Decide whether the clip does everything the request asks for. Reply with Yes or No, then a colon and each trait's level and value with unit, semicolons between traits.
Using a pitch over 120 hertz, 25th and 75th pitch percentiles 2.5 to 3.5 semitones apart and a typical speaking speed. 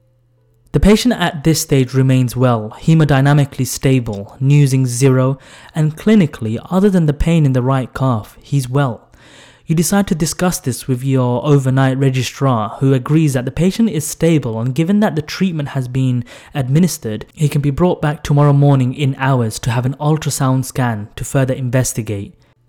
Yes: low, 135 Hz; average, 3.2 semitones; average, 170 wpm